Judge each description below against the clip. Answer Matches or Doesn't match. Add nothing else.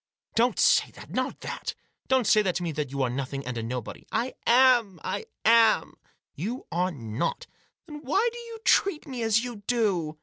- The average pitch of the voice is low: Doesn't match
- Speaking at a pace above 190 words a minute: Matches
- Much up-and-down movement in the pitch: Matches